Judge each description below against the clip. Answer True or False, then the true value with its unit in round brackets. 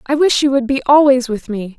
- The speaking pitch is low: False (260 Hz)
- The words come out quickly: True (270 wpm)